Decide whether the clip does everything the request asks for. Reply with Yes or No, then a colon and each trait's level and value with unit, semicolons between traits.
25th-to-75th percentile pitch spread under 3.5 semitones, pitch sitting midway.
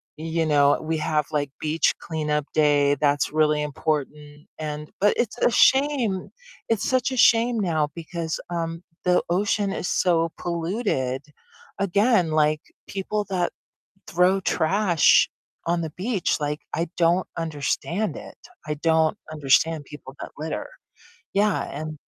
No: average, 4.1 semitones; medium, 165 Hz